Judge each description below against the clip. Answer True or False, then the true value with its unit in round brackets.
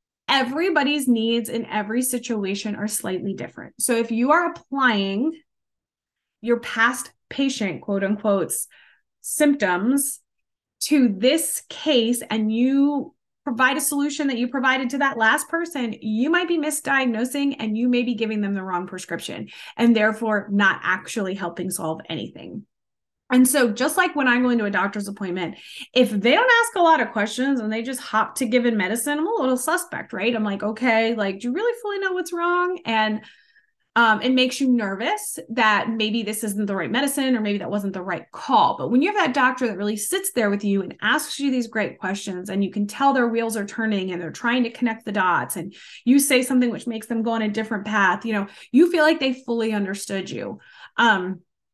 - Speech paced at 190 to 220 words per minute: True (200 wpm)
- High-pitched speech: True (235 Hz)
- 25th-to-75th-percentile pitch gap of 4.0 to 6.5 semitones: True (4.7 semitones)